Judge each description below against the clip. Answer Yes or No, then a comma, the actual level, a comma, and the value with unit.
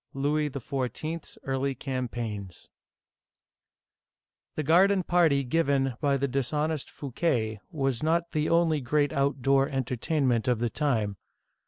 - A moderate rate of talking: No, slow, 115 wpm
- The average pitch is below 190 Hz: Yes, medium, 140 Hz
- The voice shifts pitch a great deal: No, average, 3.4 semitones